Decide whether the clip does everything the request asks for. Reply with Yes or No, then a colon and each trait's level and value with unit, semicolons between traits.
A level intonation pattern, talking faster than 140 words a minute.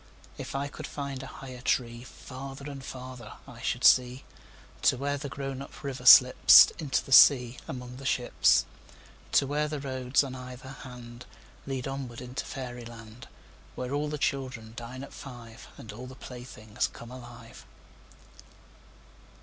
No: narrow, 1.9 semitones; slow, 135 wpm